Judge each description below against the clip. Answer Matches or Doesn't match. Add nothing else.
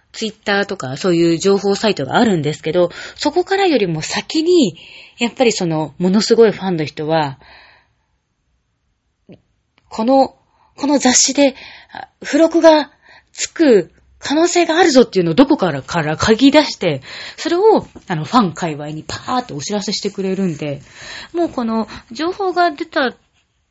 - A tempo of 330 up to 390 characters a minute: Doesn't match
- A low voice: Doesn't match